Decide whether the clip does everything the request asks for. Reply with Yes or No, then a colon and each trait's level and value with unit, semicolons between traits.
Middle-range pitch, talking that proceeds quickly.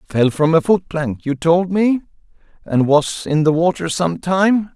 No: medium, 165 Hz; average, 190 wpm